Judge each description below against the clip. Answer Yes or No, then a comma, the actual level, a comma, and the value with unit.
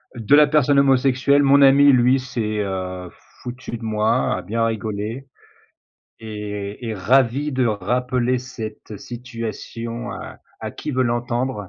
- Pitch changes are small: No, average, 3.3 semitones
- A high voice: No, low, 120 Hz